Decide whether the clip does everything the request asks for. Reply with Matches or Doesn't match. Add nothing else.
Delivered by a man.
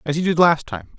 Matches